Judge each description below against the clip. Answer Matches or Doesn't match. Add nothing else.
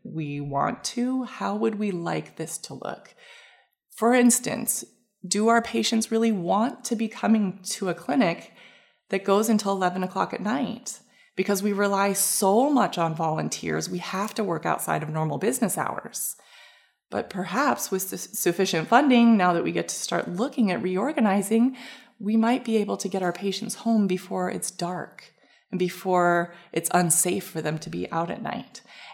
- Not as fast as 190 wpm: Matches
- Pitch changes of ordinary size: Matches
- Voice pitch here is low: Doesn't match